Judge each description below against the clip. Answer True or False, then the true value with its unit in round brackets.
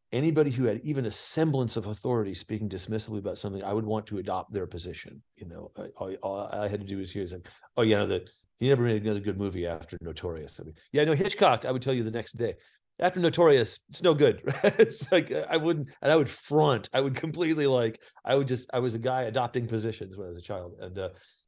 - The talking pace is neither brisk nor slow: False (250 wpm)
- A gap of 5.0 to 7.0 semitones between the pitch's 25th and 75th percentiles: True (5.3 semitones)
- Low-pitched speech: True (120 Hz)